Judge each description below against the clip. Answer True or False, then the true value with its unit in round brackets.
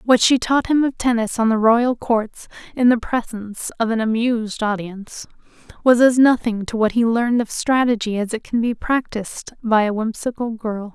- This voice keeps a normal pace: True (190 wpm)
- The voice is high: True (230 Hz)